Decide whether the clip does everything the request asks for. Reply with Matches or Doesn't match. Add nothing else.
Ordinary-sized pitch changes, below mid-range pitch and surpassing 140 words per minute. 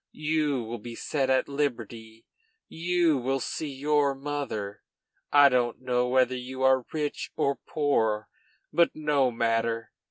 Doesn't match